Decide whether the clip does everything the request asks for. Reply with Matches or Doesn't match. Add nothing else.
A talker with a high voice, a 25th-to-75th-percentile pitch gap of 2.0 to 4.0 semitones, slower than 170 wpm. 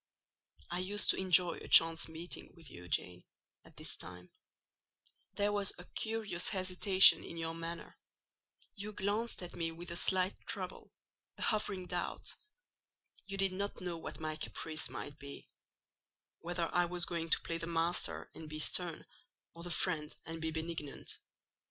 Doesn't match